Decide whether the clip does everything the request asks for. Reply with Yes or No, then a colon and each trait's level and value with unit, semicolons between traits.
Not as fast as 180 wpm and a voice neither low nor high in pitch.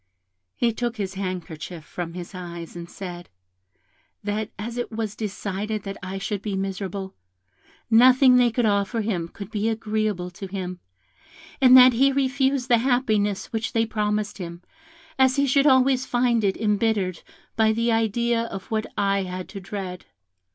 No: average, 160 wpm; high, 210 Hz